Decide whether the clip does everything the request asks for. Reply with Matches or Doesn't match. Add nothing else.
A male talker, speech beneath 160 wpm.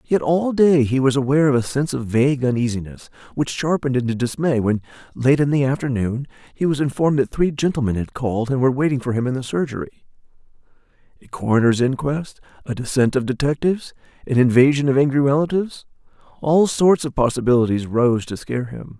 Doesn't match